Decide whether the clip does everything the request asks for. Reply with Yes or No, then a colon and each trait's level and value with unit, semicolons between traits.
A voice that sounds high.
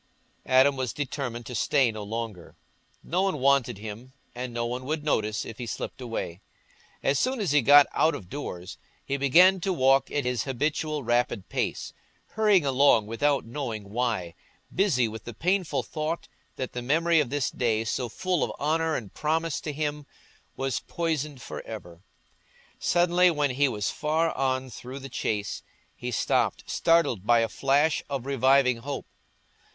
No: low, 135 Hz